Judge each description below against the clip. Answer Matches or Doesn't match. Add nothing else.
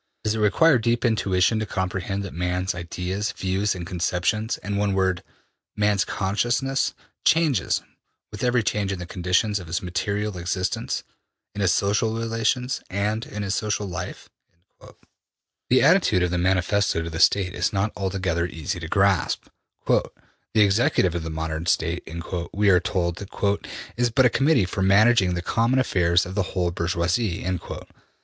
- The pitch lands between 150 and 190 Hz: Doesn't match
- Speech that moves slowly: Doesn't match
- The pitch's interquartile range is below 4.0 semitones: Matches